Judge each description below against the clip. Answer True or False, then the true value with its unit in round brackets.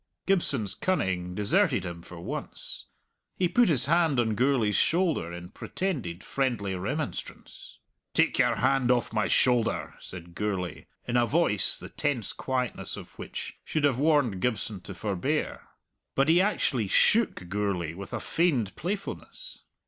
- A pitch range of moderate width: False (7.9 semitones)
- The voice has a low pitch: True (120 Hz)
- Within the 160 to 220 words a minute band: False (145 wpm)